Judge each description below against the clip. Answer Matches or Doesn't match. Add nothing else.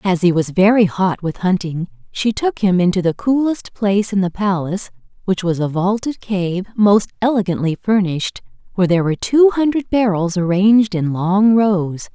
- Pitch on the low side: Doesn't match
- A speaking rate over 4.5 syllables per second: Matches